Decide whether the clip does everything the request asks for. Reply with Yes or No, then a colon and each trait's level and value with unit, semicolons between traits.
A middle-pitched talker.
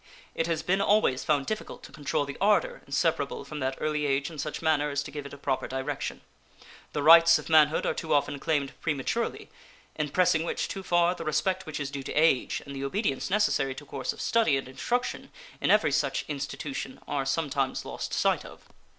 Yes: medium, 150 Hz